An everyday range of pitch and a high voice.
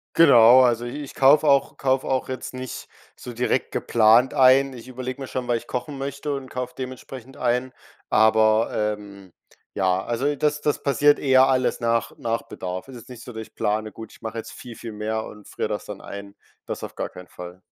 No: average, 3.2 semitones; low, 125 Hz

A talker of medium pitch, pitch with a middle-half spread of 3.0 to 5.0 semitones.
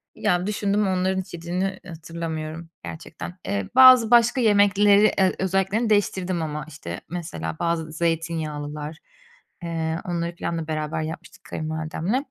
Yes: medium, 170 Hz; average, 3.4 semitones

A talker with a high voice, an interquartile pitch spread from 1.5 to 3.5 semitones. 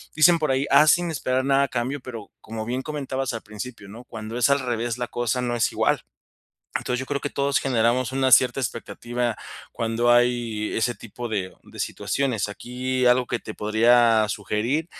No: low, 120 Hz; narrow, 2.5 semitones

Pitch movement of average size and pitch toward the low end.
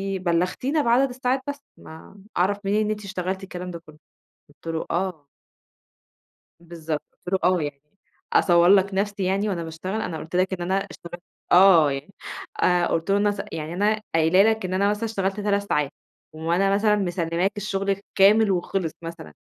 No: average, 3.0 semitones; high, 190 Hz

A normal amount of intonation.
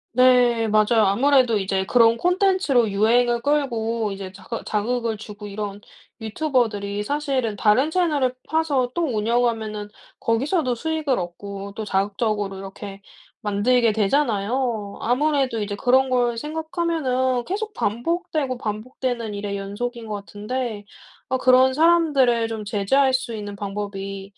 Yes: average, 4.1 semitones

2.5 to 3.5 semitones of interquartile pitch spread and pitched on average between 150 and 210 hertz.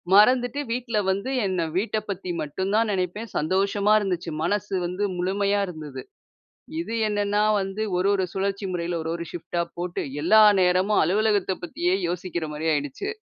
Yes: average, 2.9 semitones; high, 190 Hz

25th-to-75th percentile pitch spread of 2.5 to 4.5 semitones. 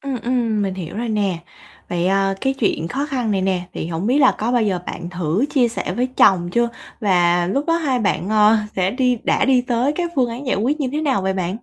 No: average, 5.3 semitones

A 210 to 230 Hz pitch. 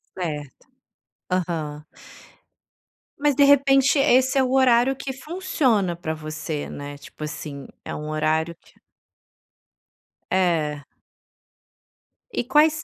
No: medium, 185 Hz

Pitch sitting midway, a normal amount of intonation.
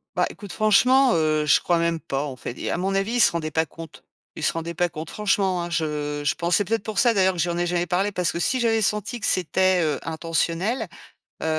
Yes: medium, 175 Hz; average, 4.0 semitones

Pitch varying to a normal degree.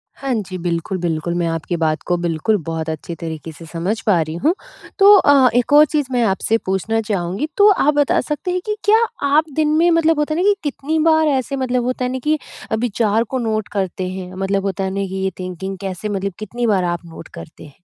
No: wide, 8.5 semitones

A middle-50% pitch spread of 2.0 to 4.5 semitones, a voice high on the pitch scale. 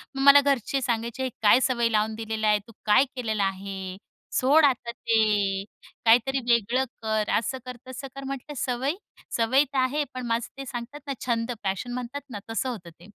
Yes: average, 3.4 semitones; high, 235 Hz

